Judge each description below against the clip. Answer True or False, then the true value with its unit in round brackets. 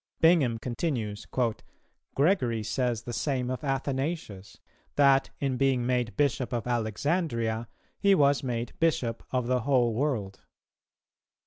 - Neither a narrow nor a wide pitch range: True (3.4 semitones)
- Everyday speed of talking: False (120 wpm)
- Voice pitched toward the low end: True (125 Hz)